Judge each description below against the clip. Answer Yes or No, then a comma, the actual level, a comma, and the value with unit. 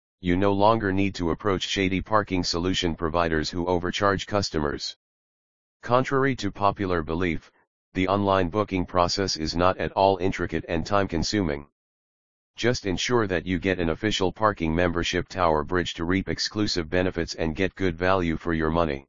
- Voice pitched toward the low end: Yes, very low, 90 Hz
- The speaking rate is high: No, average, 160 wpm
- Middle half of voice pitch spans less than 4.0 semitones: Yes, average, 2.9 semitones